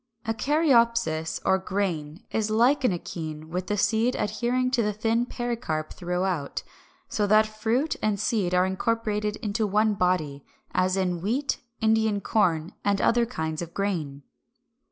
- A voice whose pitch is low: No, high, 205 Hz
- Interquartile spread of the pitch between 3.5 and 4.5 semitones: Yes, average, 4.2 semitones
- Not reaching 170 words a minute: Yes, average, 150 wpm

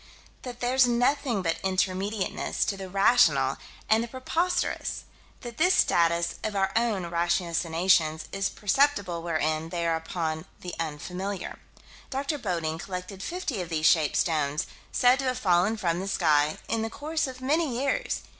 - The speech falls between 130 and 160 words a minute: Yes, average, 155 wpm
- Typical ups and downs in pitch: No, wide, 6.5 semitones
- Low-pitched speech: No, high, 195 Hz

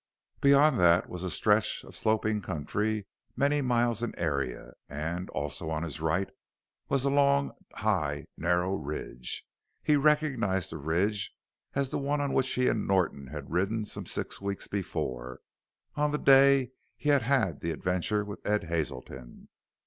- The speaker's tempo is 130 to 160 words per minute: Yes, average, 155 wpm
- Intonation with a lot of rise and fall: Yes, wide, 8.5 semitones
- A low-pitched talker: Yes, low, 100 Hz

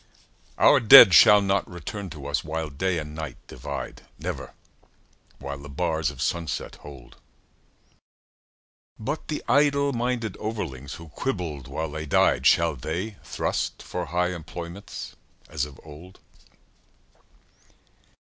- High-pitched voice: No, very low, 85 Hz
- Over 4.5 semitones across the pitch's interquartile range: Yes, wide, 5.4 semitones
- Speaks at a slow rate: Yes, slow, 125 wpm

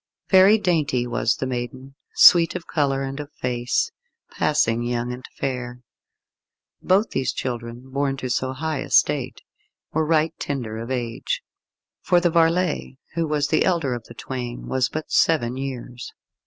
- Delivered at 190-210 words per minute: No, average, 155 wpm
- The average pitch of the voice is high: No, low, 135 Hz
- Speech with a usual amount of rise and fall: Yes, average, 4.4 semitones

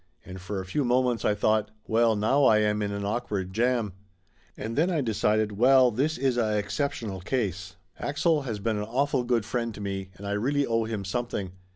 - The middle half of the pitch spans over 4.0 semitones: No, average, 3.6 semitones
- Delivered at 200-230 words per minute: Yes, fast, 205 wpm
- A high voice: No, low, 110 Hz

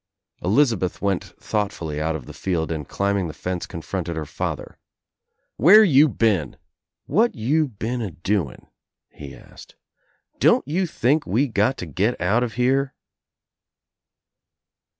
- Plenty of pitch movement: Yes, wide, 7.1 semitones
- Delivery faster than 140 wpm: No, slow, 135 wpm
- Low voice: Yes, low, 105 Hz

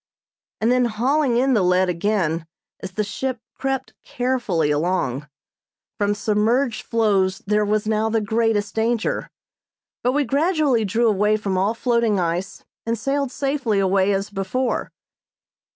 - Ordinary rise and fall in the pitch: Yes, average, 4.0 semitones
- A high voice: Yes, high, 215 Hz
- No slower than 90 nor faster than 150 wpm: Yes, average, 140 wpm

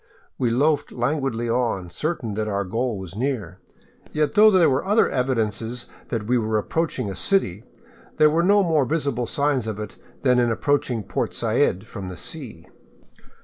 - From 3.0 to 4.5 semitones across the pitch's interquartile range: No, wide, 5.4 semitones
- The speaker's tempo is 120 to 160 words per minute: No, average, 170 wpm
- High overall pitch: No, low, 120 Hz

